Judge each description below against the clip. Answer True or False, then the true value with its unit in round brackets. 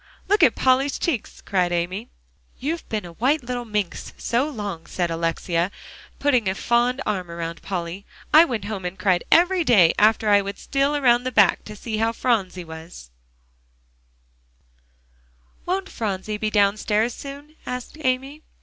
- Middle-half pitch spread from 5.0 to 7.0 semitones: True (5.6 semitones)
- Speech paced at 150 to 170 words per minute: True (160 wpm)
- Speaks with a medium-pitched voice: False (215 Hz)